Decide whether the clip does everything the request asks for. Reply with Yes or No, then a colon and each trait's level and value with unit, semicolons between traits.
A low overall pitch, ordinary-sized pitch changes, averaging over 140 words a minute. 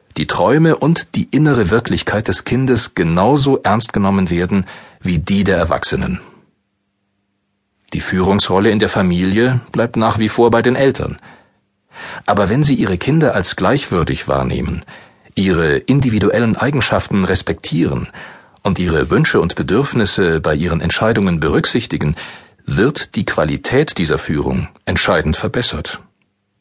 No: low, 105 Hz; average, 3.7 semitones; slow, 125 wpm